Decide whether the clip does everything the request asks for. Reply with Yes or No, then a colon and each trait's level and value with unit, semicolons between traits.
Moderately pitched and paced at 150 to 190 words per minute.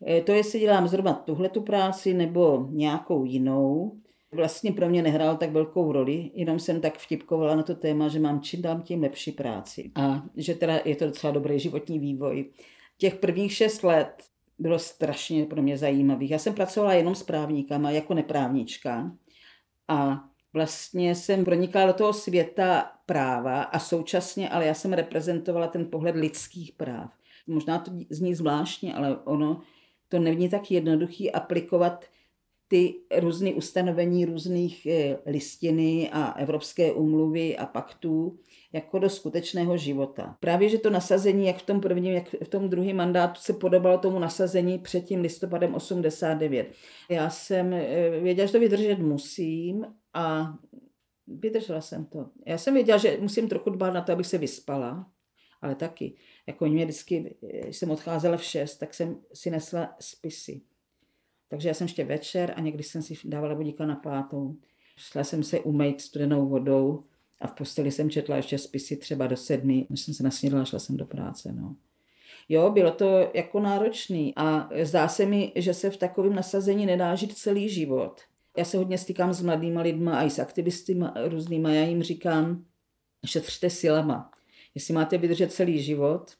Yes: medium, 165 Hz; average, 165 wpm